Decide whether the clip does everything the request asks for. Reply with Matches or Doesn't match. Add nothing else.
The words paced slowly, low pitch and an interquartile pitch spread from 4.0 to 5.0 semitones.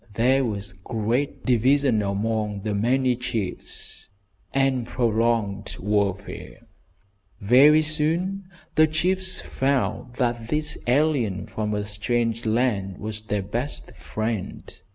Matches